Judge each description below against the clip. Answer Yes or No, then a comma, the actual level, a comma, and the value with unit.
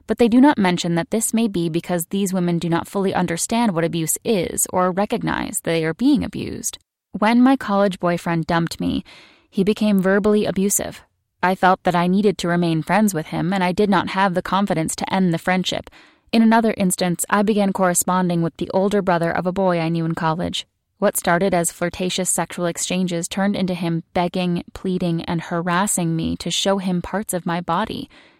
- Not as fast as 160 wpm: No, average, 200 wpm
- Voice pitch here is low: No, medium, 185 Hz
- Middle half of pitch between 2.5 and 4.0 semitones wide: Yes, average, 2.9 semitones